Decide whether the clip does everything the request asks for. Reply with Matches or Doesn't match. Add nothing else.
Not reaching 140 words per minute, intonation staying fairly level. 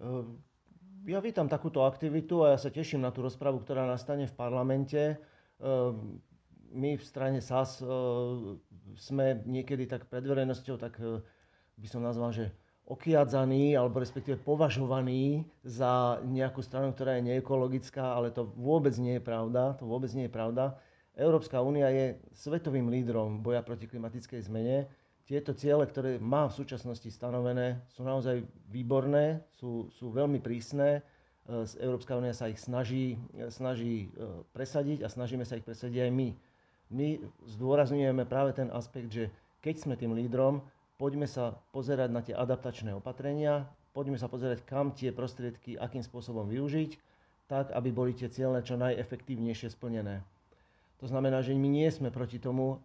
Doesn't match